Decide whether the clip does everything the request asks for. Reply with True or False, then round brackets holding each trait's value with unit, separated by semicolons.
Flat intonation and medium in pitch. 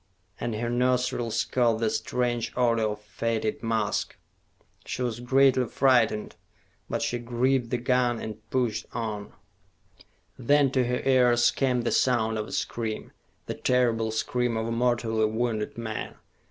False (2.0 semitones; 120 Hz)